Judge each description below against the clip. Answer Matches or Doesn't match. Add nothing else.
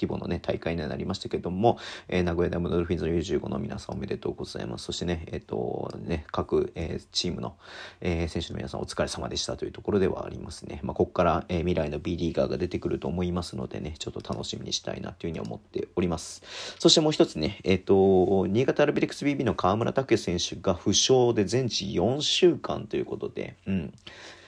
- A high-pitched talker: Doesn't match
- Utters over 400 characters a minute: Matches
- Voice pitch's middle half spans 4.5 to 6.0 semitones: Doesn't match